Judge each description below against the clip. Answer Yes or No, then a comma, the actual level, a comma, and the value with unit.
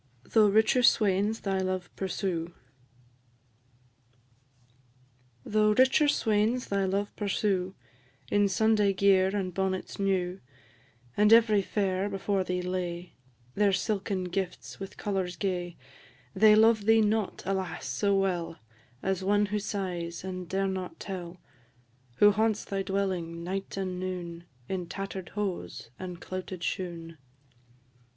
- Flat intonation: Yes, narrow, 2.2 semitones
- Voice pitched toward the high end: Yes, high, 195 Hz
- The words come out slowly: Yes, slow, 125 wpm